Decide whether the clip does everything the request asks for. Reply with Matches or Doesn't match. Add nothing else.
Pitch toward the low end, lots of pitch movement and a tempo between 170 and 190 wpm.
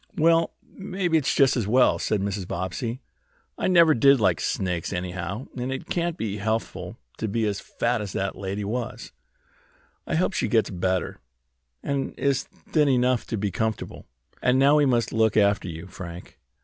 Matches